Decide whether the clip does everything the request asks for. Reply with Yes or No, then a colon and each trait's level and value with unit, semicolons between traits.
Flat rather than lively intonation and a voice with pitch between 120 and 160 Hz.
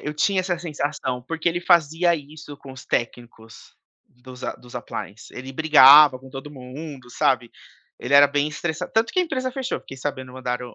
No: average, 4.0 semitones; medium, 140 Hz